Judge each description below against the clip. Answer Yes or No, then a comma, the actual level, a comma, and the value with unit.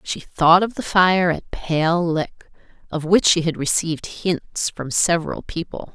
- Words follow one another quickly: No, average, 170 wpm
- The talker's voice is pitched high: No, medium, 170 Hz